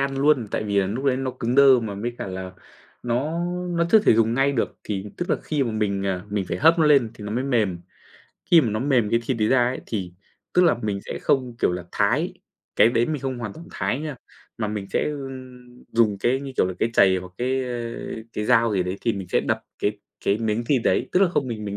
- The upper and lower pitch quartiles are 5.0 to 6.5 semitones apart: No, average, 4.5 semitones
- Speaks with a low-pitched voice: Yes, low, 120 Hz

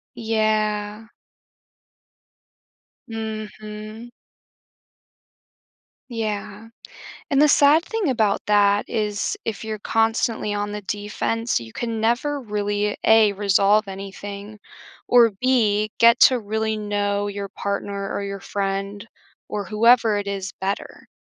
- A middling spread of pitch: No, narrow, 1.8 semitones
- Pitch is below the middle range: No, high, 210 Hz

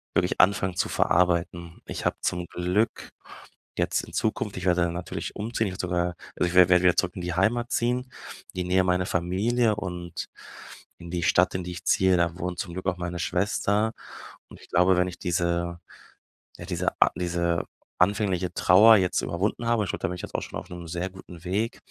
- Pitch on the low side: Yes, very low, 90 Hz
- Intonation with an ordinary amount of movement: No, narrow, 1.9 semitones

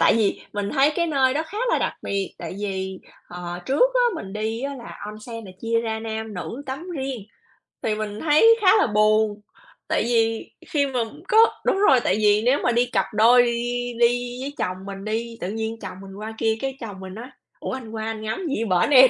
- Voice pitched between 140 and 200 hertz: No, high, 225 Hz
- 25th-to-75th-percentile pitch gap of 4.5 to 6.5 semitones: No, average, 3.8 semitones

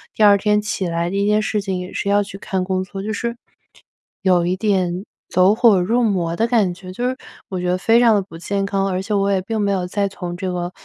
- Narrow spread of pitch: Yes, narrow, 2.3 semitones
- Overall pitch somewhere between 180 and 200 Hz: Yes, high, 195 Hz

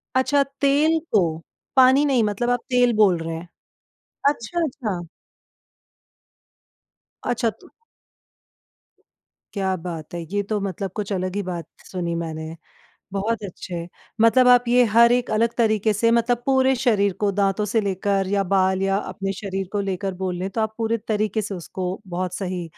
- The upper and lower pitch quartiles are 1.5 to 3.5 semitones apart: No, average, 4.0 semitones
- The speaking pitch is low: No, high, 205 Hz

